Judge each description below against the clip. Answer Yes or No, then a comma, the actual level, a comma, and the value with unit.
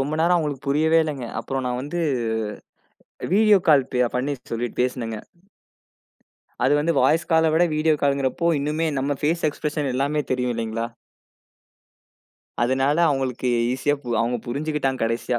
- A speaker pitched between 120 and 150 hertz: Yes, medium, 140 Hz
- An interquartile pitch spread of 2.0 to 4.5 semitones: Yes, average, 3.4 semitones